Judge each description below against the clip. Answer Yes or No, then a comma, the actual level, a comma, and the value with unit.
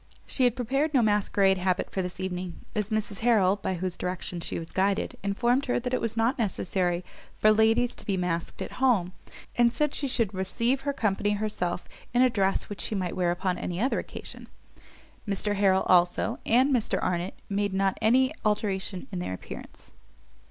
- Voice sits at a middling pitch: No, high, 200 Hz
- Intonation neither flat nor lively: Yes, average, 4.2 semitones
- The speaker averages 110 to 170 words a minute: No, average, 185 wpm